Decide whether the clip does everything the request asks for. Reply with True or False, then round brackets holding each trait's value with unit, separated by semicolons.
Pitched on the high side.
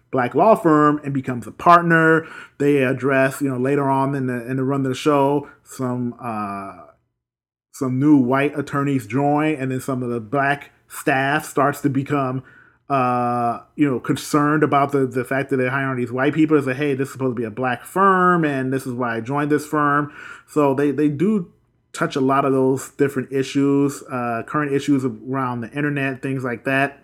False (135 Hz)